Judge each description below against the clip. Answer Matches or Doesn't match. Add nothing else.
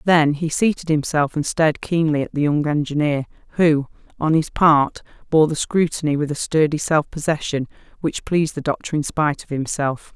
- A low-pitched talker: Doesn't match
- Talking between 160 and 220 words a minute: Matches